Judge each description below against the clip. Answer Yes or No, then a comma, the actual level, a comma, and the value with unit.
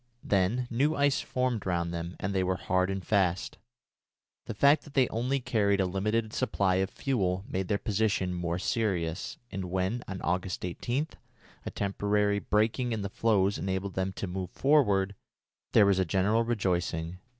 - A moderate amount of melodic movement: Yes, average, 3.7 semitones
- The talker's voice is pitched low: Yes, low, 100 Hz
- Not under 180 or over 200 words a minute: No, average, 170 wpm